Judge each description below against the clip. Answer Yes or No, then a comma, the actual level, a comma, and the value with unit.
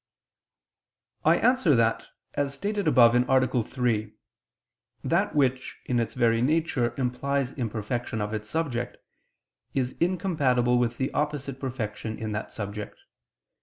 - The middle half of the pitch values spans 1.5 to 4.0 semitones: Yes, average, 3.4 semitones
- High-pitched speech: No, low, 125 Hz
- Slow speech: Yes, slow, 125 wpm